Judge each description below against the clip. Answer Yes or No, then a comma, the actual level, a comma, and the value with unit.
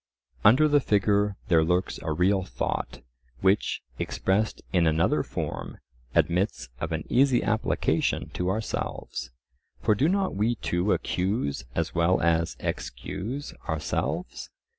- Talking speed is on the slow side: Yes, slow, 125 wpm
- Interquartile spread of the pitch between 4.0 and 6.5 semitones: Yes, average, 4.6 semitones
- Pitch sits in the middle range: No, very low, 95 Hz